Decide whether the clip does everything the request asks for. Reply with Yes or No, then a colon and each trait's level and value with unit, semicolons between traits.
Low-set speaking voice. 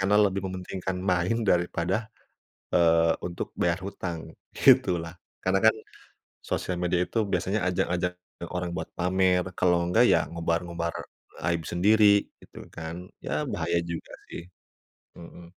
Yes: very low, 90 Hz